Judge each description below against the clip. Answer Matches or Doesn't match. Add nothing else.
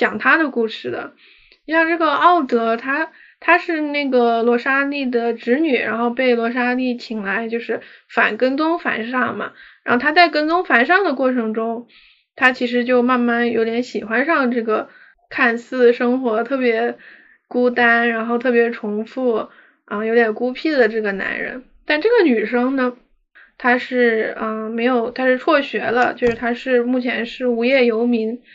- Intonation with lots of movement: Doesn't match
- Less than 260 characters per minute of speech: Matches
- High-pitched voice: Matches